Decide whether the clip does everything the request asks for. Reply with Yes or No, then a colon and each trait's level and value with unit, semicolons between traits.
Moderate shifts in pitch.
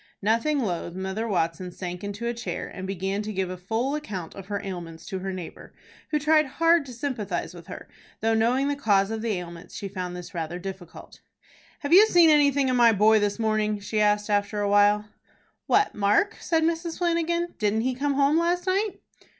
No: wide, 6.9 semitones